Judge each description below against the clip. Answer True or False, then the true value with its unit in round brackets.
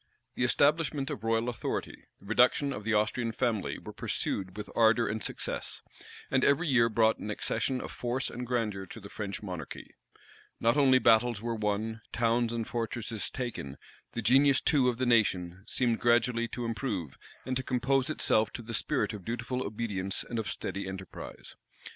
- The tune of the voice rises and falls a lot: False (2.8 semitones)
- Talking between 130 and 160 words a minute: False (175 wpm)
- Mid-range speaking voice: False (115 Hz)